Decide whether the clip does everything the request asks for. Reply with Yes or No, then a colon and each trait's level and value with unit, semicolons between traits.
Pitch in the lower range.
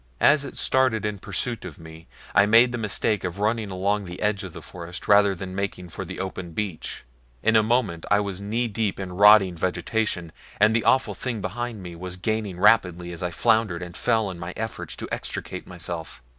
Yes: low, 100 Hz